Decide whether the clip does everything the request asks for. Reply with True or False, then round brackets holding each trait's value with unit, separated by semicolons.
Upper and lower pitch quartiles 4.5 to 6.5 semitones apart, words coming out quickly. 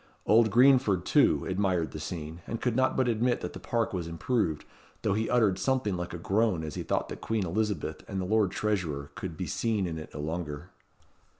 True (5.1 semitones; 210 wpm)